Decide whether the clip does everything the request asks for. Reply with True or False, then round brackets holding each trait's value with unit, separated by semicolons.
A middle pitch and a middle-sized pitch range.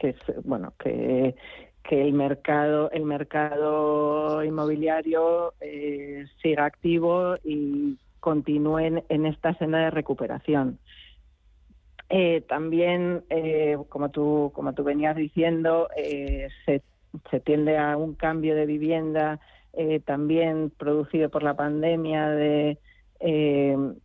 False (150 Hz; 1.6 semitones)